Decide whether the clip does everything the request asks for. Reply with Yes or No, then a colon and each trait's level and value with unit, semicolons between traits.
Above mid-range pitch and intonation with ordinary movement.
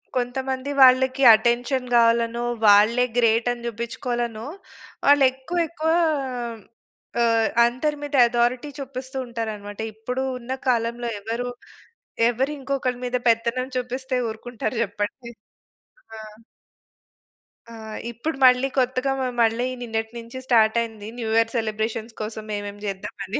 No: high, 240 Hz; narrow, 2.3 semitones